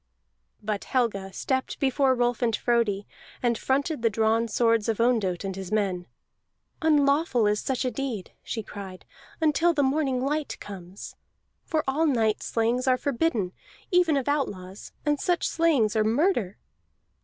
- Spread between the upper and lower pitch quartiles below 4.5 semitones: No, average, 5.2 semitones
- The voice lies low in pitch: No, high, 240 Hz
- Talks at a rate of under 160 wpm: Yes, average, 150 wpm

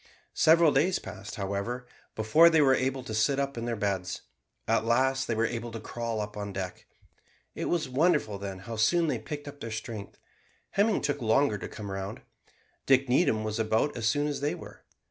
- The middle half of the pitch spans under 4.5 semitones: No, average, 4.8 semitones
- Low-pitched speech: Yes, low, 115 Hz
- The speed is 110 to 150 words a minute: No, average, 200 wpm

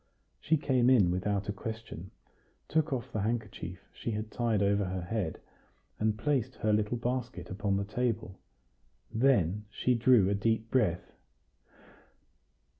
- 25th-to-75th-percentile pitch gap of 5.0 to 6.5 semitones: No, average, 3.5 semitones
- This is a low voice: Yes, low, 110 Hz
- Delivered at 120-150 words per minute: Yes, average, 140 wpm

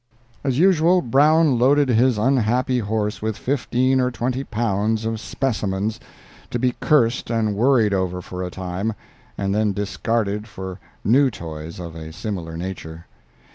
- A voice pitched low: Yes, low, 110 Hz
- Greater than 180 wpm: No, average, 145 wpm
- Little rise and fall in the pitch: No, average, 4.8 semitones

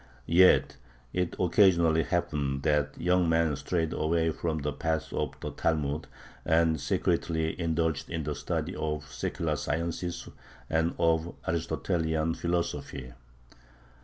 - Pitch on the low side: Yes, very low, 80 Hz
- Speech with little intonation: Yes, narrow, 1.6 semitones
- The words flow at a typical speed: No, slow, 120 wpm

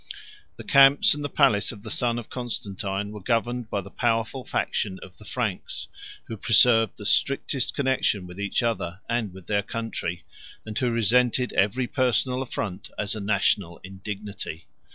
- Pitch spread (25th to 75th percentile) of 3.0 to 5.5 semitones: Yes, average, 3.7 semitones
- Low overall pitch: Yes, low, 110 Hz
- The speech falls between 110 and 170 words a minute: Yes, average, 165 wpm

